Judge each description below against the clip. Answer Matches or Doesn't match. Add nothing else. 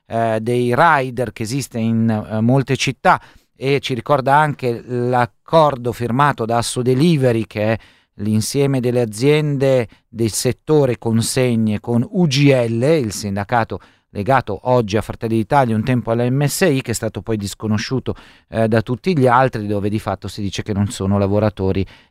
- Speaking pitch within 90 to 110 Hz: Doesn't match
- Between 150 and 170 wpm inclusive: Matches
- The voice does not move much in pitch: Doesn't match